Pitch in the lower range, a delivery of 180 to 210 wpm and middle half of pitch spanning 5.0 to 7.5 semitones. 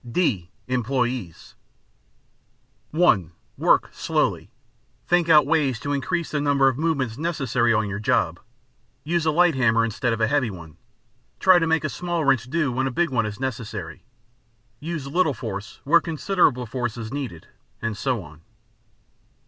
No: low, 130 Hz; average, 155 wpm; wide, 5.6 semitones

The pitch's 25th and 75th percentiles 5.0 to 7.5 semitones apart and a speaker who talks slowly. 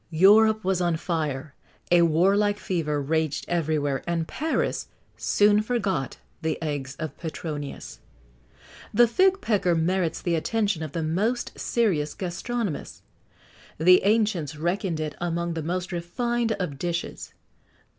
No: average, 4.6 semitones; slow, 125 wpm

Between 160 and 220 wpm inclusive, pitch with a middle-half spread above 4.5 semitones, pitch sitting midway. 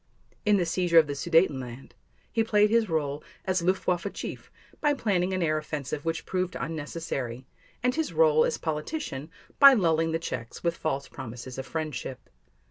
Yes: average, 165 wpm; average, 4.9 semitones; medium, 165 Hz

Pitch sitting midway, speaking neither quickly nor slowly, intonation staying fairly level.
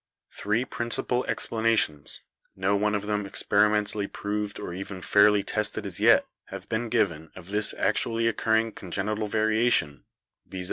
No: low, 105 Hz; average, 145 wpm; narrow, 1.8 semitones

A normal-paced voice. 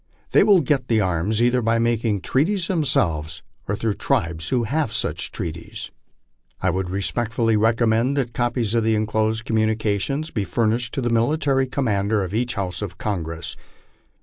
Yes: average, 160 wpm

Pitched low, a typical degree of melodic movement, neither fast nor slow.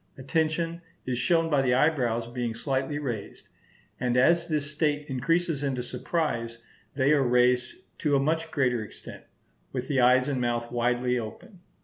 Yes: low, 130 Hz; average, 3.6 semitones; average, 155 wpm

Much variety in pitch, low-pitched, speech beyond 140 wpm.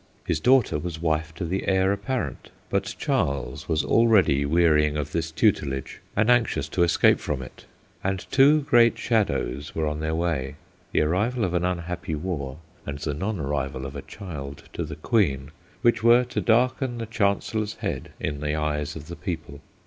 Yes: wide, 6.2 semitones; very low, 85 Hz; average, 180 wpm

